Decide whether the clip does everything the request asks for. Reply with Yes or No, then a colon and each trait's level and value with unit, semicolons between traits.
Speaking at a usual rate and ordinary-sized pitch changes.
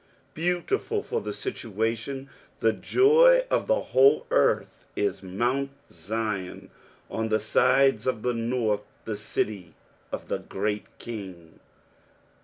No: slow, 120 wpm; average, 4.8 semitones